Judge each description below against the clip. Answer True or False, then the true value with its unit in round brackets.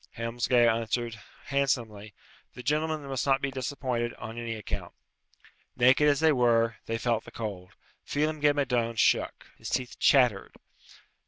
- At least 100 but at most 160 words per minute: True (150 wpm)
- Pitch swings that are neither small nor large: True (3.2 semitones)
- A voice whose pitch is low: True (120 Hz)